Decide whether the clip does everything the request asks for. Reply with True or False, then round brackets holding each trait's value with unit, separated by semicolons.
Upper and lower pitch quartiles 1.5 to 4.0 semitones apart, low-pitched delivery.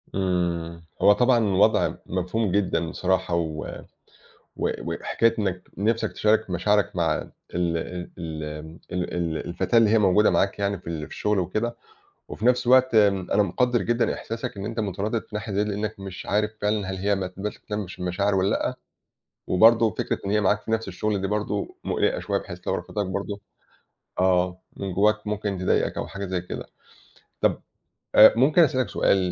True (2.9 semitones; 100 Hz)